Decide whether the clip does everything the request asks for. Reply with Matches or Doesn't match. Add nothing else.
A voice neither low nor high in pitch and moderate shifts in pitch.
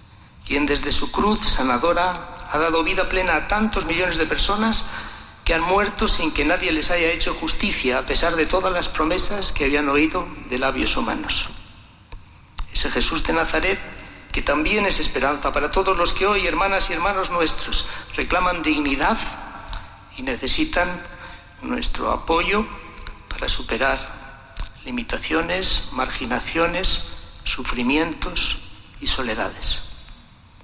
Matches